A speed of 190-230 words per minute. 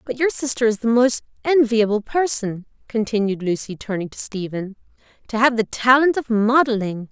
No: average, 160 wpm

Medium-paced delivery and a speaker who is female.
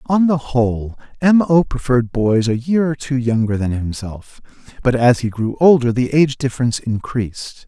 No: average, 180 wpm; male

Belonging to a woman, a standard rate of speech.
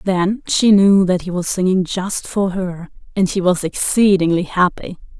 Yes: female; average, 175 wpm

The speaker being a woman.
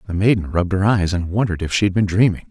No: male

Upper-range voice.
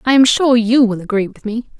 Yes: high, 230 Hz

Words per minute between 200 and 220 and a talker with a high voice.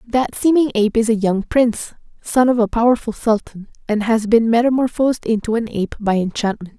No: average, 185 wpm; high, 225 Hz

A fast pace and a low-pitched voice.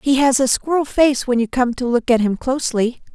No: fast, 250 wpm; very high, 255 Hz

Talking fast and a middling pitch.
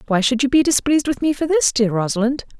No: fast, 280 wpm; very high, 255 Hz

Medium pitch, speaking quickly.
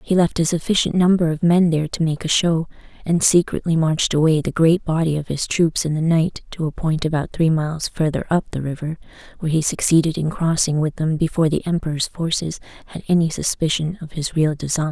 Yes: medium, 160 Hz; fast, 215 wpm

